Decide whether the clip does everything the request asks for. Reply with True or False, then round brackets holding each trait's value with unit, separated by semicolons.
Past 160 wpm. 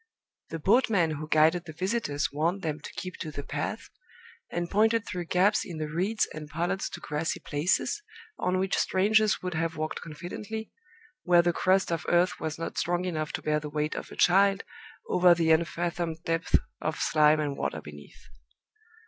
True (180 wpm)